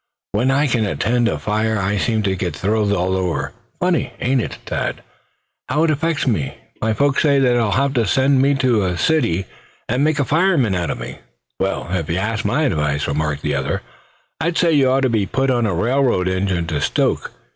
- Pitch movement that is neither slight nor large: No, wide, 6.5 semitones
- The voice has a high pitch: No, low, 115 Hz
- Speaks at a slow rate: No, fast, 205 wpm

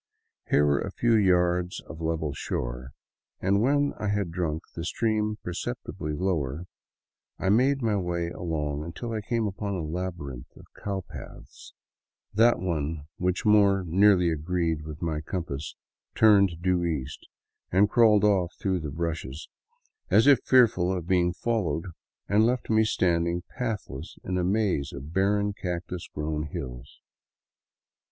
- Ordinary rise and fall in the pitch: Yes, average, 4.3 semitones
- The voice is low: Yes, very low, 90 Hz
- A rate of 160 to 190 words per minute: No, average, 145 wpm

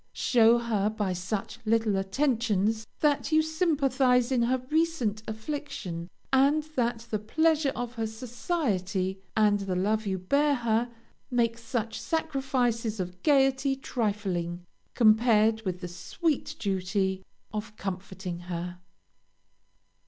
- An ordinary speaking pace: No, slow, 120 wpm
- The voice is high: Yes, high, 225 Hz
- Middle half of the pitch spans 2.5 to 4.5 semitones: No, average, 5.2 semitones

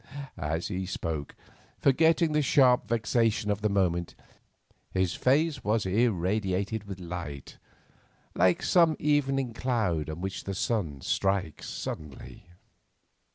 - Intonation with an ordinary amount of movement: No, wide, 6.0 semitones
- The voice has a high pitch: No, low, 100 Hz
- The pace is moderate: No, slow, 110 wpm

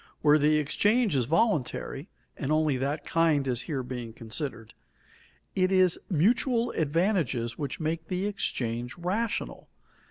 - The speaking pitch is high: No, medium, 155 Hz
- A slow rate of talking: Yes, slow, 130 wpm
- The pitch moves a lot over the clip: Yes, wide, 6.0 semitones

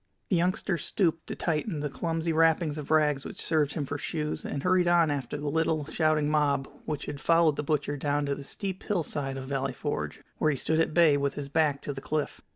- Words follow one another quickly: Yes, fast, 225 wpm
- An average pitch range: No, narrow, 2.3 semitones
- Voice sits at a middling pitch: Yes, medium, 150 Hz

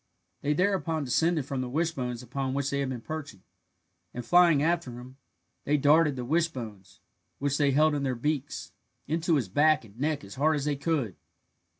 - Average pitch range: Yes, average, 3.7 semitones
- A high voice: No, medium, 140 Hz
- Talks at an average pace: Yes, average, 185 wpm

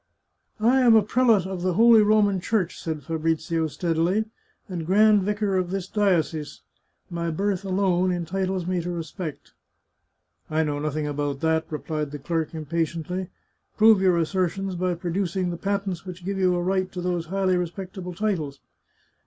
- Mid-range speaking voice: Yes, medium, 180 Hz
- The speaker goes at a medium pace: Yes, average, 175 wpm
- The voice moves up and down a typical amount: Yes, average, 3.0 semitones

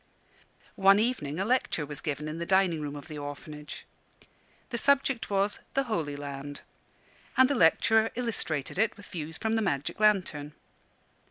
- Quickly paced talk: No, average, 160 wpm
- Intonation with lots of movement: Yes, wide, 7.0 semitones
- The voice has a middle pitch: Yes, medium, 175 Hz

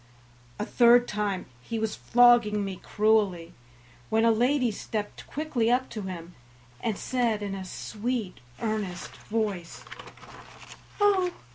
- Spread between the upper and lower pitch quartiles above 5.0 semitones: No, average, 3.3 semitones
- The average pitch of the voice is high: Yes, high, 220 Hz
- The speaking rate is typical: No, slow, 125 wpm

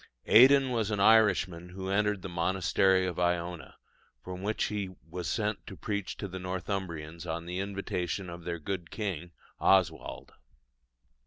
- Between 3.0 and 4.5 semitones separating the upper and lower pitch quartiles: No, narrow, 2.6 semitones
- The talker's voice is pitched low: Yes, very low, 95 Hz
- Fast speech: No, average, 150 wpm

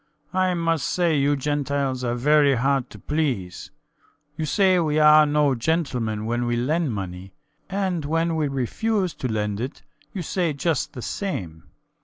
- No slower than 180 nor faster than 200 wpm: No, average, 160 wpm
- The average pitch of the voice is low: No, medium, 145 Hz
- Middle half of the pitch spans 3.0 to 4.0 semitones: No, average, 5.3 semitones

